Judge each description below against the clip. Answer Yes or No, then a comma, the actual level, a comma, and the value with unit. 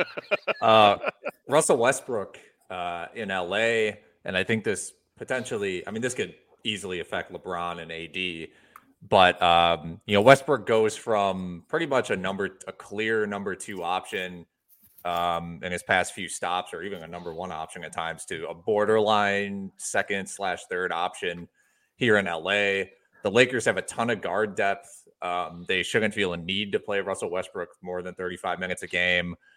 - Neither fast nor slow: Yes, average, 160 wpm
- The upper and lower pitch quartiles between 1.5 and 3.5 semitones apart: Yes, average, 2.9 semitones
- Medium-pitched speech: No, very low, 90 Hz